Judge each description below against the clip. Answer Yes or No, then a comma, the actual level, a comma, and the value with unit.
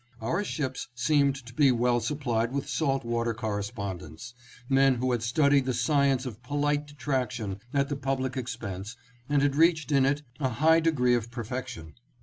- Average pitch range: Yes, average, 3.4 semitones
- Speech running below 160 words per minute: No, average, 170 wpm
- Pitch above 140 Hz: No, low, 130 Hz